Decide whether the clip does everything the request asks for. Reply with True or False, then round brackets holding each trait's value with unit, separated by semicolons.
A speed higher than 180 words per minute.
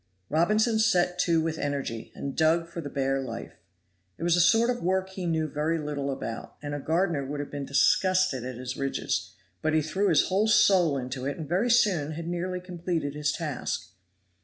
True (200 wpm)